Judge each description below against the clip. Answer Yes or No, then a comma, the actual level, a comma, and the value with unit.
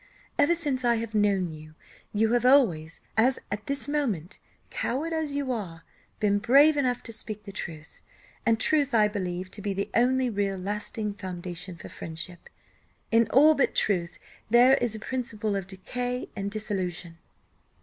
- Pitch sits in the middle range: No, high, 215 Hz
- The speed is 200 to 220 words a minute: No, average, 165 wpm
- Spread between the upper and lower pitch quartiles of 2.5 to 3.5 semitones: No, average, 5.1 semitones